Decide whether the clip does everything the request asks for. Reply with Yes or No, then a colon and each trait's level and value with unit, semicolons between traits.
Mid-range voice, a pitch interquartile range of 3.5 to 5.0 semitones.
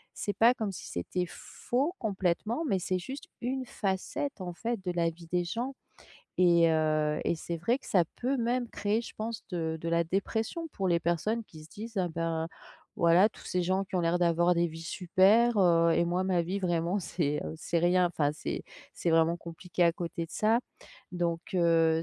Yes: medium, 180 Hz; average, 4.1 semitones